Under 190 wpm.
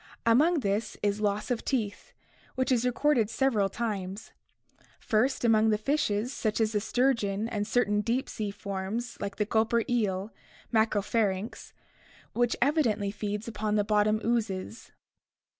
Yes: average, 140 wpm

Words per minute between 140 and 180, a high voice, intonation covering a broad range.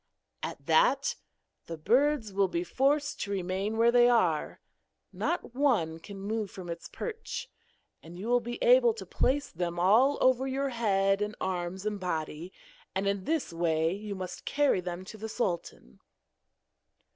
Yes: average, 160 wpm; high, 205 Hz; wide, 6.3 semitones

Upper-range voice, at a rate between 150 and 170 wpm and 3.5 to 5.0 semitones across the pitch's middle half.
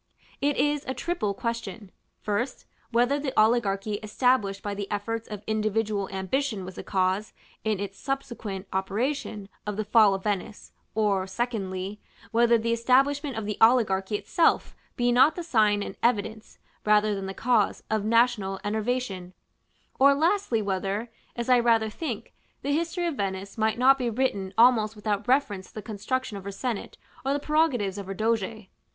Yes: high, 220 Hz; average, 165 wpm; average, 3.8 semitones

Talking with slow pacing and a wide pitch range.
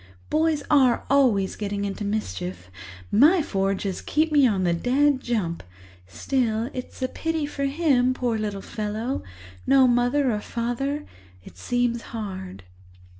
Yes: slow, 130 wpm; wide, 5.8 semitones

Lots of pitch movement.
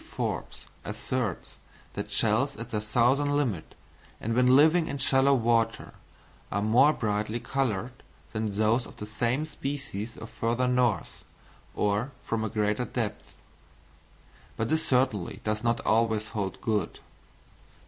No: average, 3.4 semitones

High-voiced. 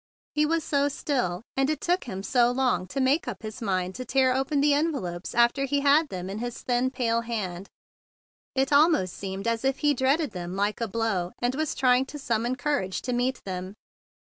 Yes: high, 245 Hz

